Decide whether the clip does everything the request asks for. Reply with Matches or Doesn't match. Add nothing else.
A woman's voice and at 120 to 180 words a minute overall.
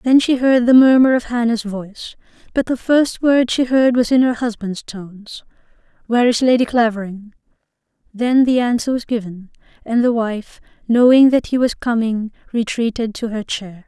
Matches